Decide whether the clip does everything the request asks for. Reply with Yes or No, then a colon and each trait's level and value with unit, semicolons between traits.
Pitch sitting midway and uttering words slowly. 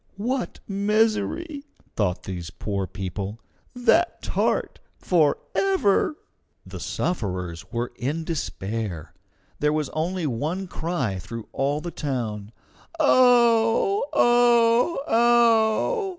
Yes: medium, 175 Hz; slow, 95 wpm